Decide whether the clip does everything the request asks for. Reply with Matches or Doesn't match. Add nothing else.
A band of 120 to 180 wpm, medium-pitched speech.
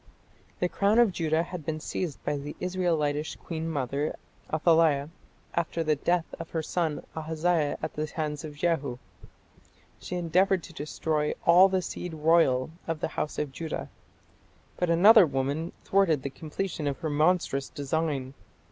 Matches